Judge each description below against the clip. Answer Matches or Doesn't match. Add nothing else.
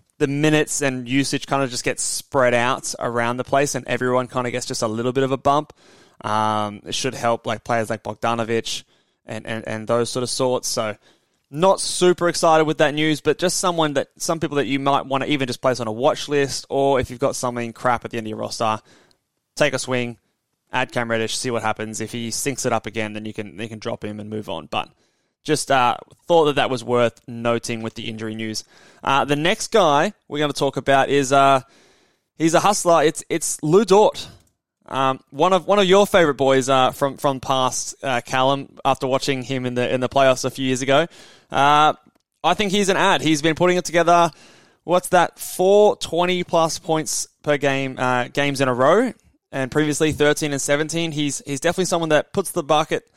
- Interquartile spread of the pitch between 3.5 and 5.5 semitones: Matches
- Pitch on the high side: Doesn't match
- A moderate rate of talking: Doesn't match